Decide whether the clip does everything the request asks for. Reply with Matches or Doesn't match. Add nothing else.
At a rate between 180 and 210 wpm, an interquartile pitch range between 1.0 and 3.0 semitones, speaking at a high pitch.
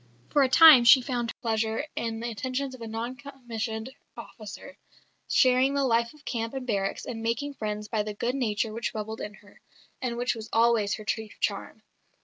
Matches